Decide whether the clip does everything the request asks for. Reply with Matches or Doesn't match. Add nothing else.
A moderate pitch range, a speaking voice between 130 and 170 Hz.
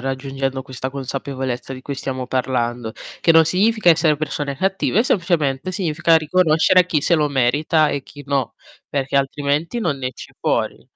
Matches